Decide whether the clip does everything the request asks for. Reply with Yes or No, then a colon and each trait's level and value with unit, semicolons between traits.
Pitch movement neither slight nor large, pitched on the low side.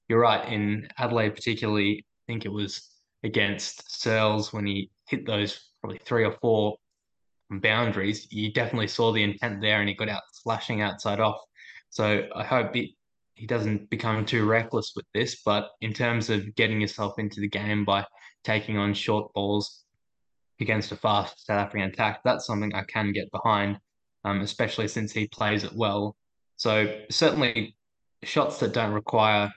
No: narrow, 1.4 semitones; low, 105 Hz